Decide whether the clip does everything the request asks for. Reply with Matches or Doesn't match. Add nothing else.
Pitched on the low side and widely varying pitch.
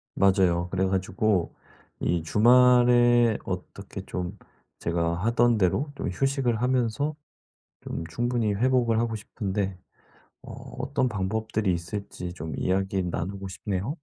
Doesn't match